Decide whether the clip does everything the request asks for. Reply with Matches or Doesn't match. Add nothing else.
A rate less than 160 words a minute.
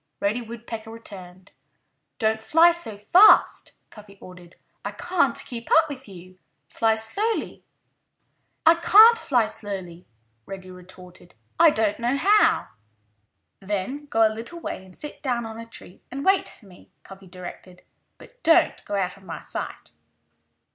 Matches